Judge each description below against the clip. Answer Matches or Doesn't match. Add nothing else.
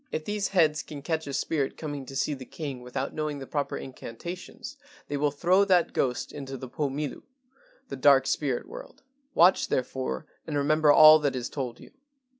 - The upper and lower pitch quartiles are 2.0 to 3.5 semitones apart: Matches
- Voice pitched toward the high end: Doesn't match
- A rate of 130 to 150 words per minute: Doesn't match